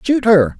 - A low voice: No, high, 190 Hz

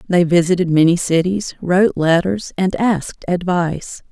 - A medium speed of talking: No, slow, 130 wpm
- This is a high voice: No, medium, 175 Hz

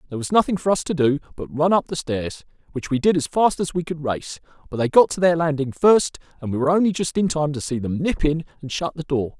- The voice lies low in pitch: No, medium, 155 Hz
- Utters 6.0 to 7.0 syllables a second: Yes, 6.1 syllables/s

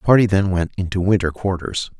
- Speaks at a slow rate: No, fast, 210 wpm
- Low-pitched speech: Yes, very low, 95 Hz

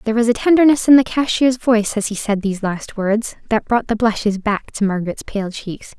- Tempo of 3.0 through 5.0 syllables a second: No, 5.6 syllables/s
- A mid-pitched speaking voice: No, high, 220 Hz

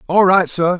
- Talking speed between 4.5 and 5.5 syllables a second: Yes, 4.9 syllables/s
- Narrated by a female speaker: No, male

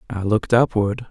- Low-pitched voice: Yes, low, 105 Hz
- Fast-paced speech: No, average, 165 wpm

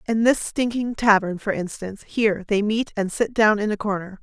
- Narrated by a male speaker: No, female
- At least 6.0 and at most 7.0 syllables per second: No, 5.3 syllables/s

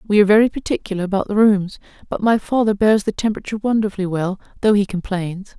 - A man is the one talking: No, female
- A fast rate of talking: No, average, 195 wpm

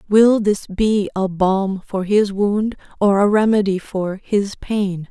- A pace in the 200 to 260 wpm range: No, average, 165 wpm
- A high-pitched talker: Yes, high, 200 Hz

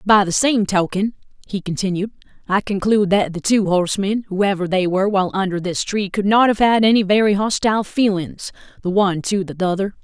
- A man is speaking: No, female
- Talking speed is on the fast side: No, average, 190 wpm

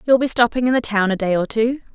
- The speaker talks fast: Yes, fast, 310 wpm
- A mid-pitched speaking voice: No, high, 230 Hz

